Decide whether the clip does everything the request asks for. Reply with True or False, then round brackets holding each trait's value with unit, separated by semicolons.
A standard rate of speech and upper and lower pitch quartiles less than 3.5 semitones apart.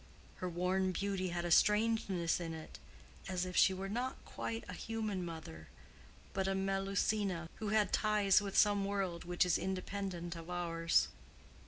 True (160 wpm; 2.6 semitones)